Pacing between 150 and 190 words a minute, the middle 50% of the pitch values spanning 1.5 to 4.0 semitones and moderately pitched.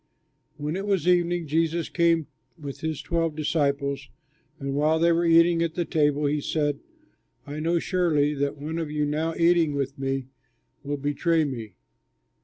Yes: average, 165 wpm; narrow, 2.6 semitones; medium, 155 Hz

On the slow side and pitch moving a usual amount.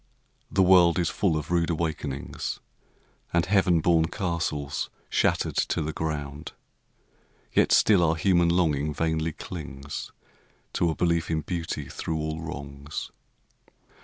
No: slow, 130 wpm; narrow, 2.2 semitones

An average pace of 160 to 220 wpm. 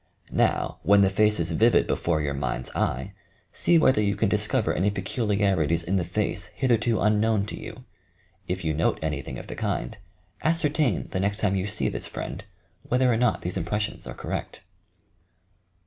Yes: average, 180 wpm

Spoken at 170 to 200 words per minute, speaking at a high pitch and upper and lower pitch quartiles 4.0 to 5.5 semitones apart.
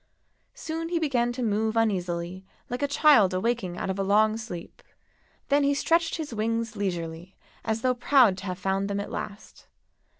Yes: average, 175 wpm; high, 220 Hz; average, 4.8 semitones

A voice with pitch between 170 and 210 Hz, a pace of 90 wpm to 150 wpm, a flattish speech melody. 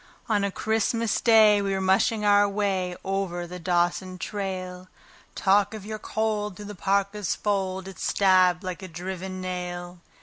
No: high, 190 Hz; average, 160 wpm; narrow, 2.1 semitones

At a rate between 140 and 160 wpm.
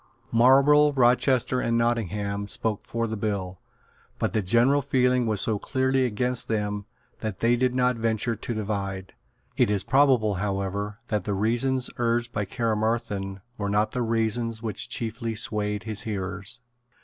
Yes: average, 150 wpm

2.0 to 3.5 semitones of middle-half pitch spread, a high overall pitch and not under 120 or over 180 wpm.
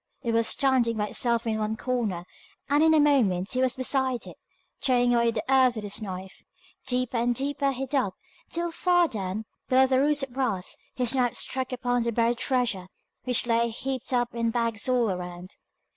No: average, 2.8 semitones; high, 245 Hz; average, 190 wpm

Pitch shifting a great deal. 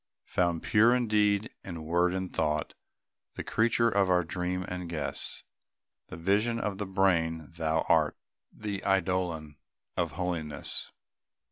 No: average, 3.6 semitones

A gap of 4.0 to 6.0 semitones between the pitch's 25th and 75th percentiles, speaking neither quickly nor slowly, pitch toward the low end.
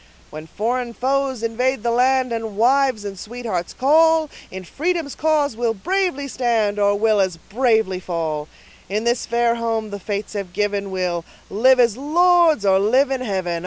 No: average, 4.7 semitones; average, 165 wpm; high, 230 Hz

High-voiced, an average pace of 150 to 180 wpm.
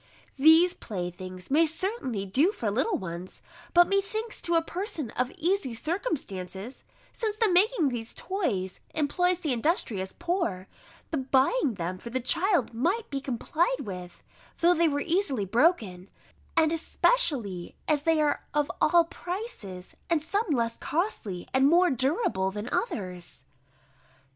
No: very high, 295 Hz; average, 140 wpm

